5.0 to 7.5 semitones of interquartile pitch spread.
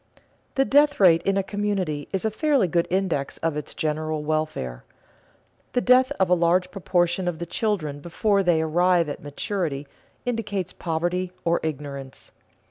No: average, 4.0 semitones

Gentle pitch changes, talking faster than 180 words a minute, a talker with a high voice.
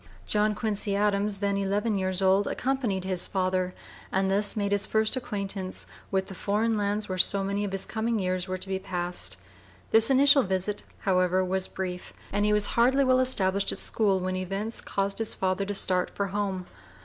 Yes: narrow, 1.9 semitones; average, 190 wpm; high, 200 Hz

